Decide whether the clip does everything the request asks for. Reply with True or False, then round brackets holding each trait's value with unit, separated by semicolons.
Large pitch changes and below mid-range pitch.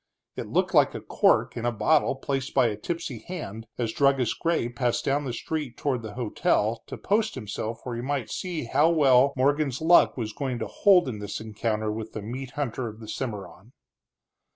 False (4.2 semitones; 125 Hz)